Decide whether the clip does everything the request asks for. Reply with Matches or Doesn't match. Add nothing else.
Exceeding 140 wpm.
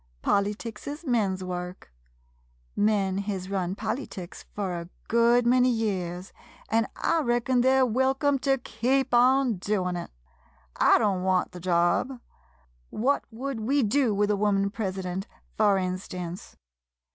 Doesn't match